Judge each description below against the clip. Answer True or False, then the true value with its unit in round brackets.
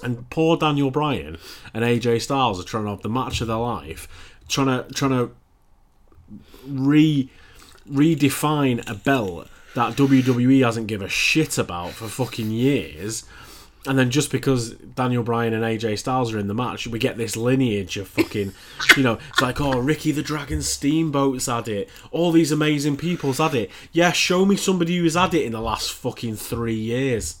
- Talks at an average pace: True (180 wpm)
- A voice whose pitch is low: True (125 Hz)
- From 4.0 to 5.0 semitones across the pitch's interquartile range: True (4.3 semitones)